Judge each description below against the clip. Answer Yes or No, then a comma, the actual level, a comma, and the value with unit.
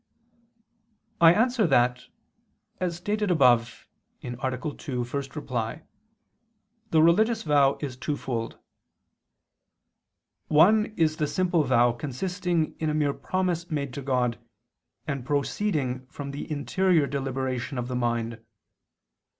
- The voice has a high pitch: No, medium, 140 Hz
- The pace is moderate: No, slow, 115 wpm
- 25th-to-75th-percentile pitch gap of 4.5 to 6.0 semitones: Yes, average, 5.1 semitones